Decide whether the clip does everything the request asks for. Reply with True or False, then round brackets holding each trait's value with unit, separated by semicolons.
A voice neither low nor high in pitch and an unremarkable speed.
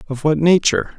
True (150 Hz; 185 wpm)